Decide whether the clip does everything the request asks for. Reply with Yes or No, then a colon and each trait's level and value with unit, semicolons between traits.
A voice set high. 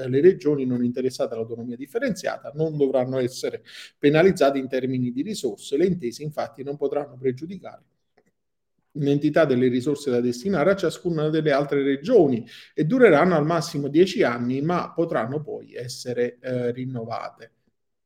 No: medium, 140 Hz